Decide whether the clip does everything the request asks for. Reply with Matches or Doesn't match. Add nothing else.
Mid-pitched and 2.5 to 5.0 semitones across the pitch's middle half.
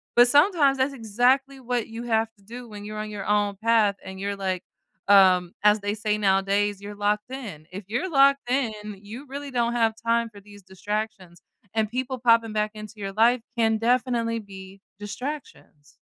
Doesn't match